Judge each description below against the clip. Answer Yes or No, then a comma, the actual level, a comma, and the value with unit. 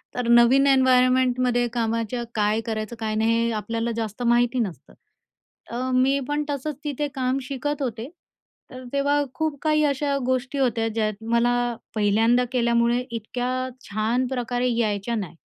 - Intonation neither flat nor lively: No, narrow, 2.3 semitones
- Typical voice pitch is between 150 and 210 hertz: No, high, 245 Hz